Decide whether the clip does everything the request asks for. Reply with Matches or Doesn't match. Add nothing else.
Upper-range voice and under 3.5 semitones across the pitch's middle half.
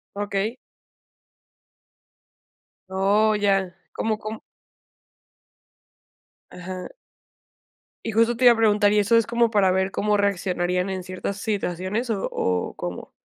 Matches